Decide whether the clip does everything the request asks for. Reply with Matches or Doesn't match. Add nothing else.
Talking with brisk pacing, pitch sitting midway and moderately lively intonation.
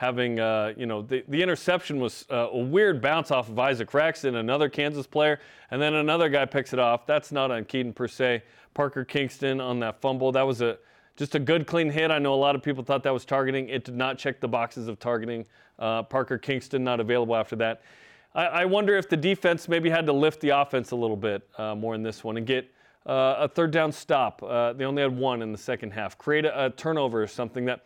Doesn't match